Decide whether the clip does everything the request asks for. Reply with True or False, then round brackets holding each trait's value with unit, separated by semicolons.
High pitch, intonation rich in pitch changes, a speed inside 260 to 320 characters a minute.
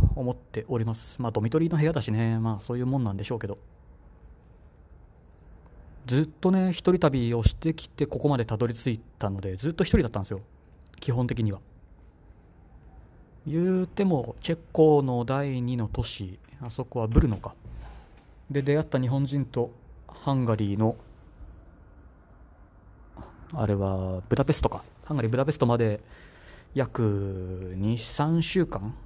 False (115 Hz; 6.0 semitones; 285 characters per minute)